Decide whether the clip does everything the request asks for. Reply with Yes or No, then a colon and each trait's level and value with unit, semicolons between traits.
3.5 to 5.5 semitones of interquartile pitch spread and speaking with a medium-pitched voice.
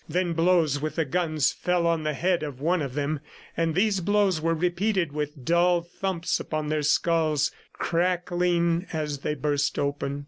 No: average, 2.9 semitones; medium, 165 Hz